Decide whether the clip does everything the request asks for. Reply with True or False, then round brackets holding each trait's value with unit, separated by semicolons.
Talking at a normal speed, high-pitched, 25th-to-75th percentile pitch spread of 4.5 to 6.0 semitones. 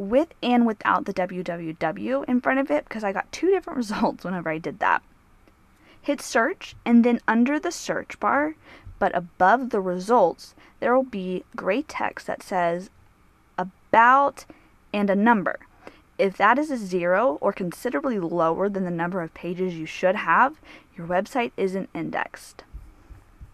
True (160 wpm; 200 Hz; 5.6 semitones)